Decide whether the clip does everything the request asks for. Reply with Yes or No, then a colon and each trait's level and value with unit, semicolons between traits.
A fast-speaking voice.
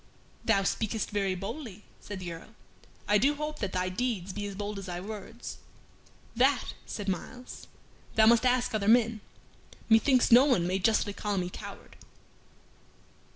No: average, 155 wpm